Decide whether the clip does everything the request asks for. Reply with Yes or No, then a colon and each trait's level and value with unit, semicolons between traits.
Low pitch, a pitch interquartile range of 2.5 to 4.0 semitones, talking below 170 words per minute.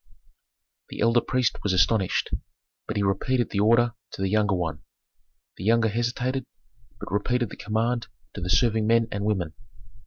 Yes: low, 110 Hz; average, 3.2 semitones; average, 160 wpm